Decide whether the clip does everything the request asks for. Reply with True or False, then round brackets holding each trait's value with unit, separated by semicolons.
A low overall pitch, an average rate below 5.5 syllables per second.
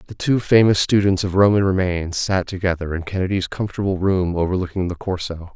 False (95 Hz; 5.8 syllables/s)